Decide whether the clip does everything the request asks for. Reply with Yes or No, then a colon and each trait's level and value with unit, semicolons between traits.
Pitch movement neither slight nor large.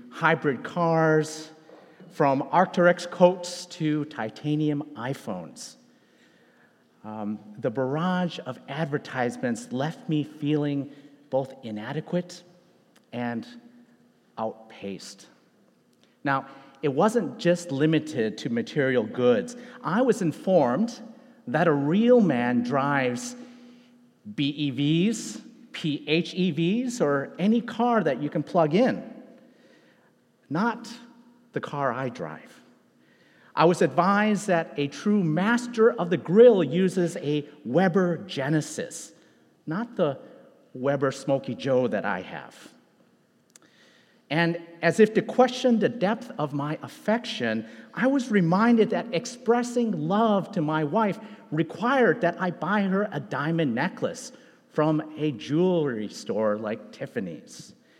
No: wide, 7.9 semitones